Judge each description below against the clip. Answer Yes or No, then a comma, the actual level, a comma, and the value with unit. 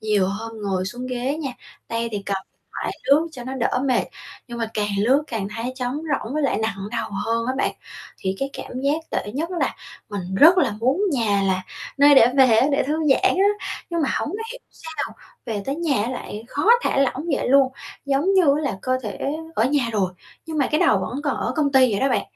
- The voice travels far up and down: No, average, 4.7 semitones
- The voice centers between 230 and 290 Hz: Yes, very high, 255 Hz